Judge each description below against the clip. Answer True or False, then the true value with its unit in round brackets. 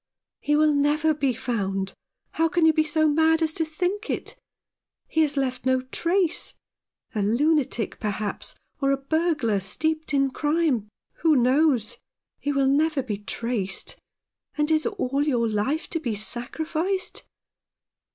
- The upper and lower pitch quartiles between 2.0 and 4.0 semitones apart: False (4.7 semitones)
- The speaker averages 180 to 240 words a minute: False (150 wpm)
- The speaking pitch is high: True (290 Hz)